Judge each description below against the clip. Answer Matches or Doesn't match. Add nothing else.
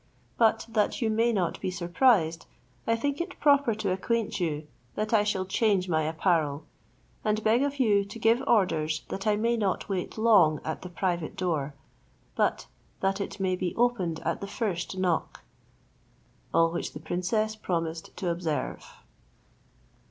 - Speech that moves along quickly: Doesn't match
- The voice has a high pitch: Matches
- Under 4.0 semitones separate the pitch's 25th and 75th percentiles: Doesn't match